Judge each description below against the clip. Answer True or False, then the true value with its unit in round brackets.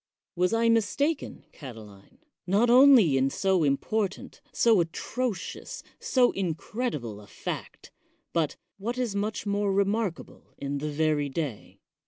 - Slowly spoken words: True (130 wpm)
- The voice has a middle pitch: False (195 Hz)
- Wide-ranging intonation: True (7.6 semitones)